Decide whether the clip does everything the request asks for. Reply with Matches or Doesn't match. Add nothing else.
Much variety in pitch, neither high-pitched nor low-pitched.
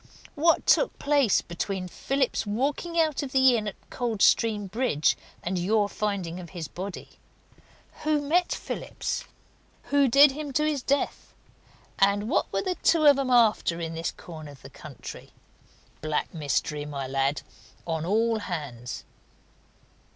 Doesn't match